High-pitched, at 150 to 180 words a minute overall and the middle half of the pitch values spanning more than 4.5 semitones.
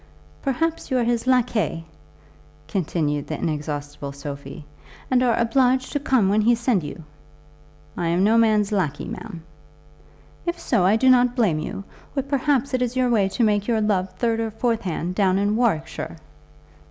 Yes: high, 220 Hz; average, 170 wpm; wide, 5.6 semitones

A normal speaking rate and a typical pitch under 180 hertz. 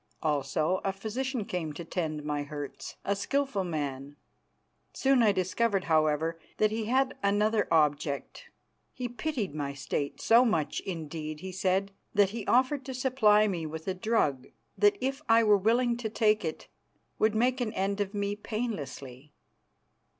No: average, 160 wpm; high, 200 Hz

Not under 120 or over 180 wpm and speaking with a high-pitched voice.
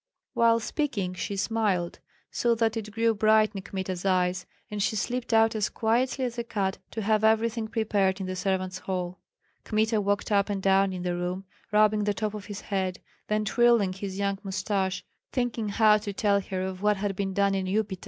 No: average, 200 wpm; high, 205 Hz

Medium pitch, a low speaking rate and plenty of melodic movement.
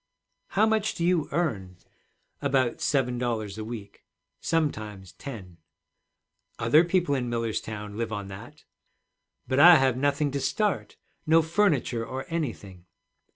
No: low, 130 Hz; slow, 130 wpm; wide, 6.6 semitones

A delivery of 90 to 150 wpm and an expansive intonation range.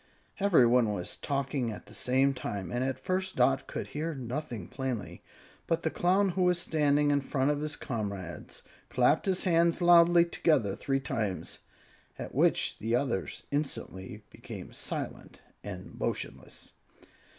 Yes: average, 145 wpm; wide, 6.0 semitones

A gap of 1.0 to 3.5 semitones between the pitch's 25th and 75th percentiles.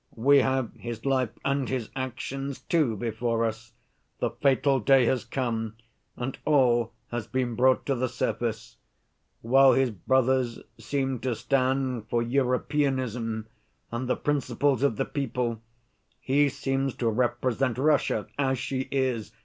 Yes: narrow, 2.4 semitones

